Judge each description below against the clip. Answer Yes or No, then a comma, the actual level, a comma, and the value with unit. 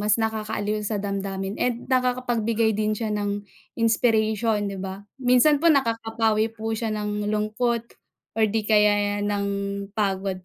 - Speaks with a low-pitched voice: No, high, 215 Hz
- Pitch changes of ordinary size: No, narrow, 1.8 semitones